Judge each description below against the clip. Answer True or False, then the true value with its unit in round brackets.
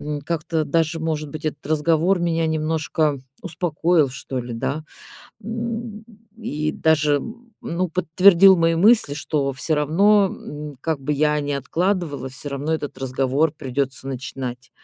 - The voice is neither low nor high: True (155 Hz)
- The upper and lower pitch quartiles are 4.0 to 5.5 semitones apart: False (3.2 semitones)